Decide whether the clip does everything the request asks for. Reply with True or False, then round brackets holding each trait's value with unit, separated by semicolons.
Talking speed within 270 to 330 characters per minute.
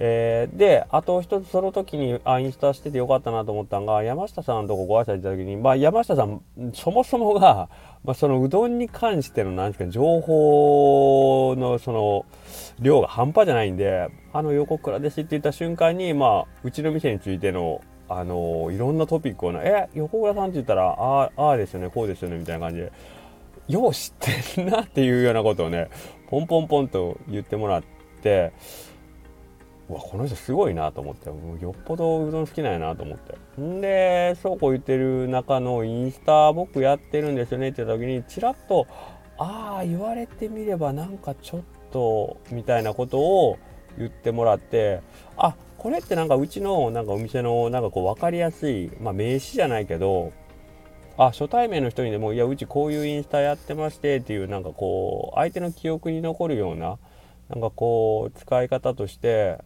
False (380 characters per minute)